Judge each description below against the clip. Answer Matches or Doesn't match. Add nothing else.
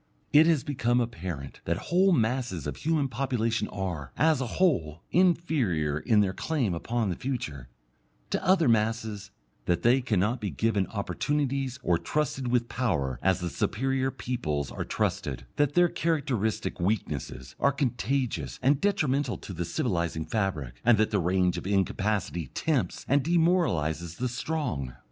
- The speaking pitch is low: Matches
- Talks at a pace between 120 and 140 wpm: Doesn't match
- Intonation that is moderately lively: Doesn't match